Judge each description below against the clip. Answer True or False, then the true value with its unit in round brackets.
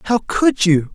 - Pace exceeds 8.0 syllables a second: False (3.9 syllables/s)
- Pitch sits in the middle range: False (205 Hz)